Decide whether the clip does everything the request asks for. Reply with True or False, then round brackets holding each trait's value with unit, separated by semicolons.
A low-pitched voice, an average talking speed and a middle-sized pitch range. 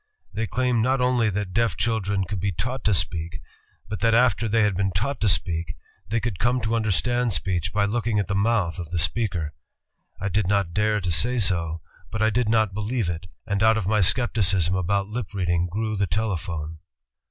False (100 Hz; 210 wpm; 4.0 semitones)